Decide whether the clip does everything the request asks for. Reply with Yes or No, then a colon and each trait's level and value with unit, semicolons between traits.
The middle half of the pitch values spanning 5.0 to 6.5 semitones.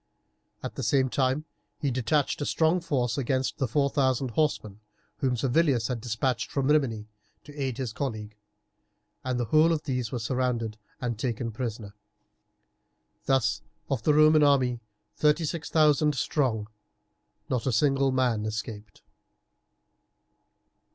No: average, 3.9 semitones